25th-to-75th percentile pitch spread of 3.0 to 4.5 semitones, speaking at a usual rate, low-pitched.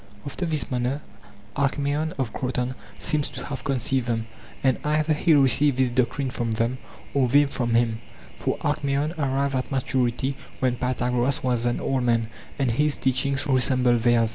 No: narrow, 2.4 semitones; average, 165 wpm; low, 130 Hz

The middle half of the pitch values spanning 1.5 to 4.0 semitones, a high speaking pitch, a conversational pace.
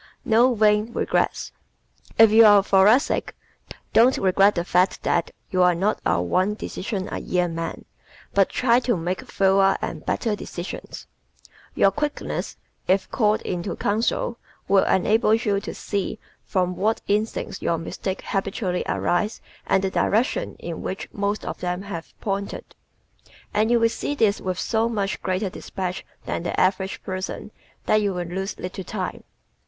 Yes: average, 2.8 semitones; high, 195 Hz; average, 160 wpm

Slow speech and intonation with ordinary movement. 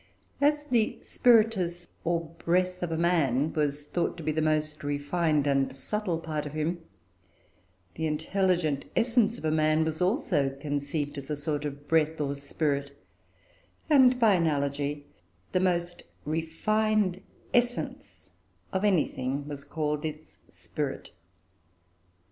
Yes: slow, 130 wpm; average, 3.8 semitones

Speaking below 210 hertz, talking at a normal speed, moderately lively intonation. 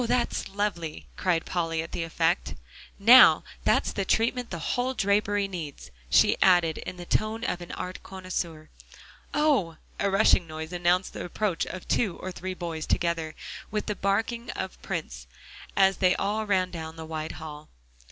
Yes: medium, 185 Hz; average, 165 wpm; average, 3.7 semitones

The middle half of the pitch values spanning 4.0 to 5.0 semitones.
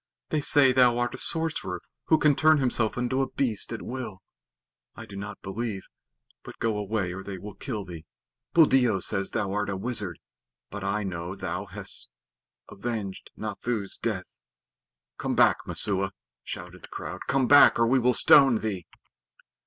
Yes: average, 4.5 semitones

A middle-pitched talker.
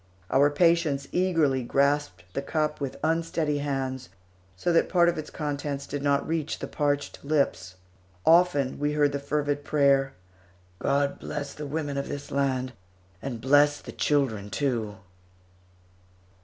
Yes: medium, 145 Hz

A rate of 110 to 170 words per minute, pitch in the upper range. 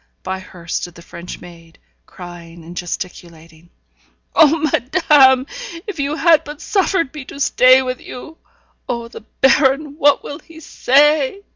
Yes: average, 145 wpm; very high, 260 Hz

